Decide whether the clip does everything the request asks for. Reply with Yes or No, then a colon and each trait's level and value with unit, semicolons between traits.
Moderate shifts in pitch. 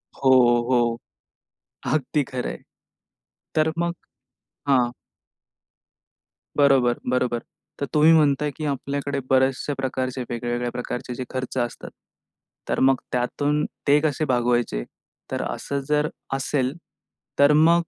Yes: average, 3.1 semitones